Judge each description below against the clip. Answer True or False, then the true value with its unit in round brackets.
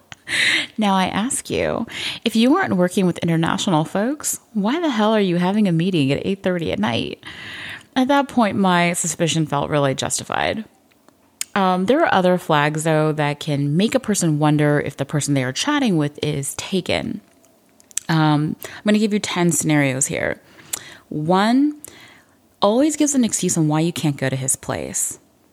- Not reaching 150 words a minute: False (175 wpm)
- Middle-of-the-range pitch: True (175 Hz)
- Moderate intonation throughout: False (5.8 semitones)